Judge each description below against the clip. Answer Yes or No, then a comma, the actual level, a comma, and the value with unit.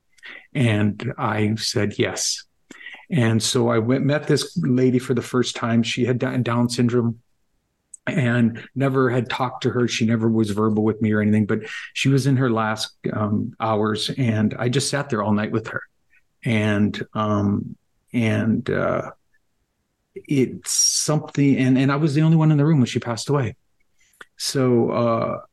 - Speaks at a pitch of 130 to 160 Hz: No, low, 120 Hz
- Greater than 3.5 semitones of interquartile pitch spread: No, average, 3.2 semitones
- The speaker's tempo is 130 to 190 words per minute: Yes, average, 170 wpm